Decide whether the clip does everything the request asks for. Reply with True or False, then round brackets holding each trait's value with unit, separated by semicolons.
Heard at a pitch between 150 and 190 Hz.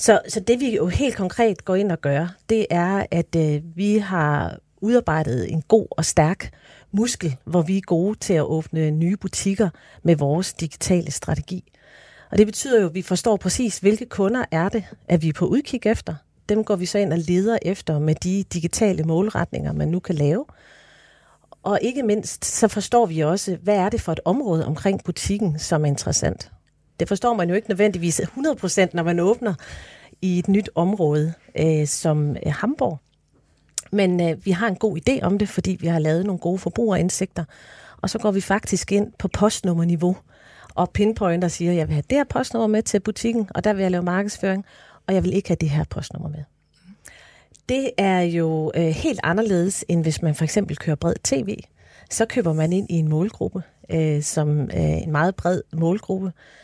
True (185 Hz)